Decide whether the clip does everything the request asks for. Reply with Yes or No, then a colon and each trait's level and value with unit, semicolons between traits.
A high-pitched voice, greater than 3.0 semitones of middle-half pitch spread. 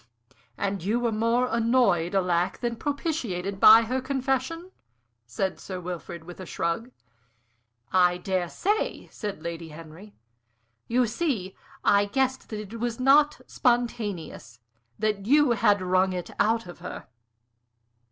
Yes: high, 210 Hz; average, 5.3 semitones